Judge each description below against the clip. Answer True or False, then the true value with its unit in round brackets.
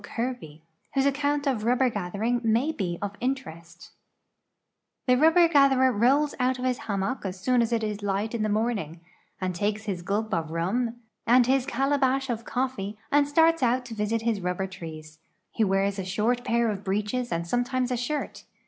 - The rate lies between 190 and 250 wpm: True (195 wpm)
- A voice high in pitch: True (230 Hz)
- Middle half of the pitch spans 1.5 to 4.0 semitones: False (4.6 semitones)